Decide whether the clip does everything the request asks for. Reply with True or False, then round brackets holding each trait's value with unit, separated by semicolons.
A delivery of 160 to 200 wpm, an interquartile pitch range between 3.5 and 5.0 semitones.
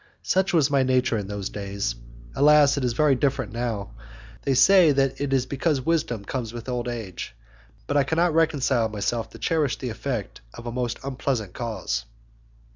True (180 wpm; 3.8 semitones)